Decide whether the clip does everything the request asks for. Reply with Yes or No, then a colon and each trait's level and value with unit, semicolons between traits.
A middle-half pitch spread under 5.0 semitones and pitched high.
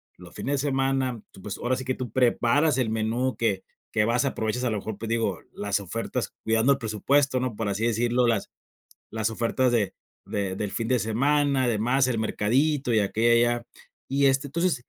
No: average, 3.0 semitones; low, 120 Hz